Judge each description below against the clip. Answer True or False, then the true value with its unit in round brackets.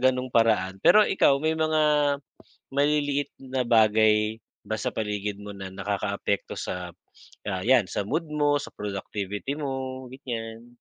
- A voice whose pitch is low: True (115 Hz)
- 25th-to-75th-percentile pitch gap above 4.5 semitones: True (5.1 semitones)